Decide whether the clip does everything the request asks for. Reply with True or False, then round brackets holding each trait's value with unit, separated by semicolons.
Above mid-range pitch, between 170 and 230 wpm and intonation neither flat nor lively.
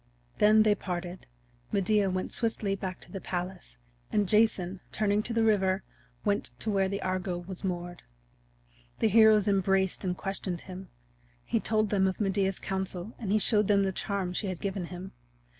False (195 Hz; 175 wpm; 2.2 semitones)